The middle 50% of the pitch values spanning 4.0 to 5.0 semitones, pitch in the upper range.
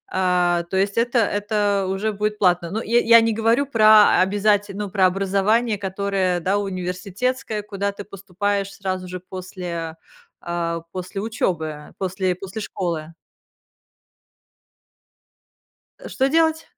No: narrow, 2.6 semitones; high, 195 Hz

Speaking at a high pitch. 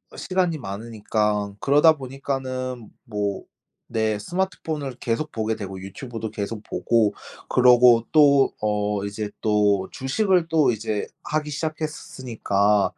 No: low, 115 Hz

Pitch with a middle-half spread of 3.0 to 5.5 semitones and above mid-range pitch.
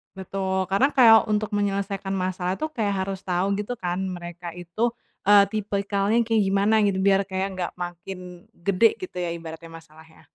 No: narrow, 2.5 semitones; high, 195 Hz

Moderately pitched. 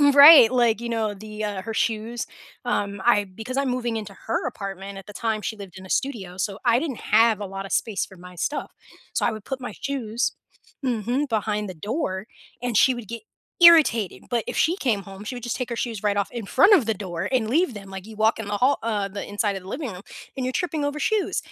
No: high, 220 Hz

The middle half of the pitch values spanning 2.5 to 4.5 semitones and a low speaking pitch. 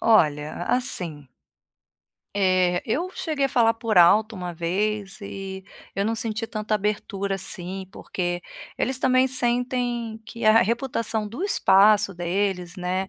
No: average, 3.8 semitones; high, 210 Hz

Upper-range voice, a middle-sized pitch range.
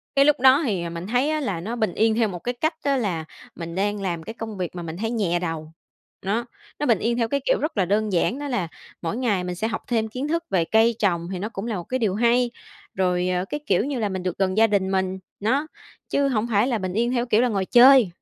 Yes: high, 215 Hz; average, 4.7 semitones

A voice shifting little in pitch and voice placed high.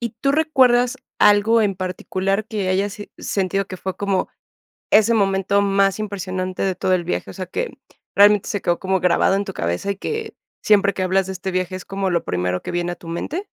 Yes: narrow, 2.0 semitones; high, 195 Hz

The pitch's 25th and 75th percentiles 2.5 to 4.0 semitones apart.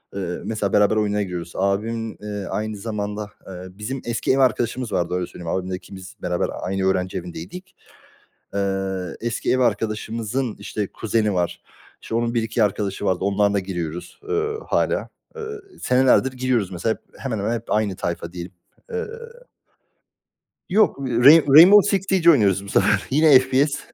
No: average, 4.8 semitones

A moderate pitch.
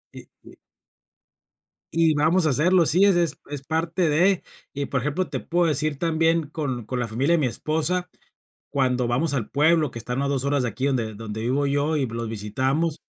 Yes: medium, 145 Hz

